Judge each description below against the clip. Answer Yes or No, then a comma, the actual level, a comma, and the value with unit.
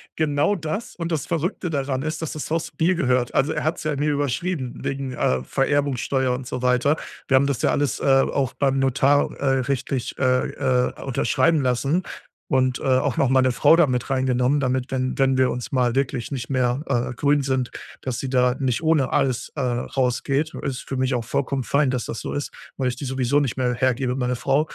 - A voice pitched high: No, low, 135 Hz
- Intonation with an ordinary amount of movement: No, narrow, 2.2 semitones